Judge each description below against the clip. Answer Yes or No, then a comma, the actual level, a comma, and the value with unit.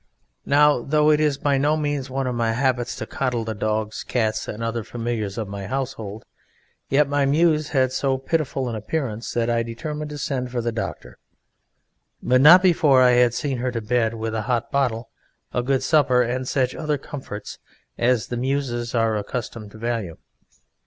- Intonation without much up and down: No, average, 3.4 semitones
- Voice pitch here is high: No, low, 125 Hz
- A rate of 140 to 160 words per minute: No, average, 185 wpm